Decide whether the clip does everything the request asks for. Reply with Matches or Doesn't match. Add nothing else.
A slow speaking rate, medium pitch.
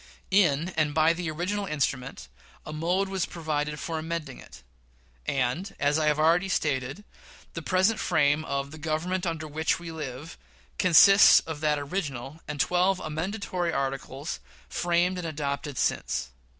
Doesn't match